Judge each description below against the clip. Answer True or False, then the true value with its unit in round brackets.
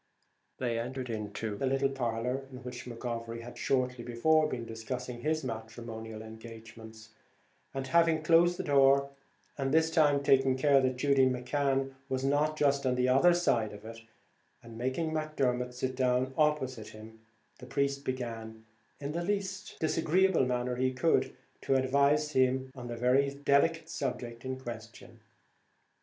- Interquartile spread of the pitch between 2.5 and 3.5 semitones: True (3.0 semitones)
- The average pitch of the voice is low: True (130 Hz)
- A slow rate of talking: False (150 wpm)